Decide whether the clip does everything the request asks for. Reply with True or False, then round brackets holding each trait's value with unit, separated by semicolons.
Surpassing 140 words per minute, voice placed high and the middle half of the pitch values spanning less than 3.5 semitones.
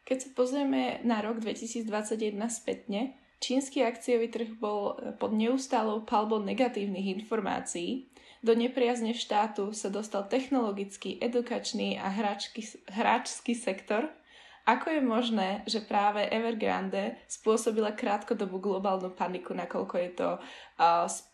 False (115 wpm; 225 Hz; 2.9 semitones)